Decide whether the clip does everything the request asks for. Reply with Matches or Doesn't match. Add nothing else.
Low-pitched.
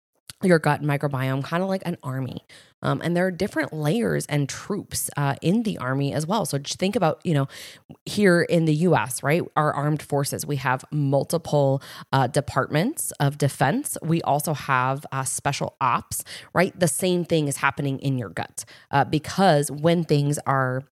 Doesn't match